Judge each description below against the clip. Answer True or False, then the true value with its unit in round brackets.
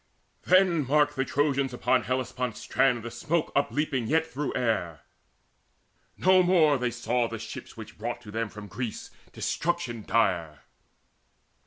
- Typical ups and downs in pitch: True (4.6 semitones)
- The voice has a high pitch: False (130 Hz)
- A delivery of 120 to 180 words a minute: True (140 wpm)